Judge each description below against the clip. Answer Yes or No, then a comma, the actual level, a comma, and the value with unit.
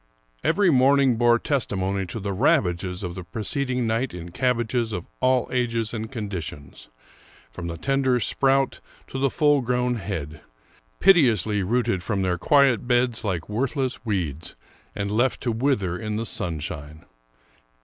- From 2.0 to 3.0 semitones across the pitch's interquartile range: No, wide, 5.4 semitones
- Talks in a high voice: No, low, 115 Hz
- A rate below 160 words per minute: Yes, average, 150 wpm